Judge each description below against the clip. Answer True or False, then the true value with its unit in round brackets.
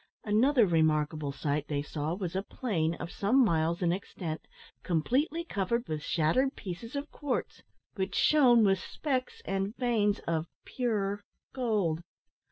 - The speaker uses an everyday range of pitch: False (6.9 semitones)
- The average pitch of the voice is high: True (195 Hz)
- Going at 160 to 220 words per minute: False (140 wpm)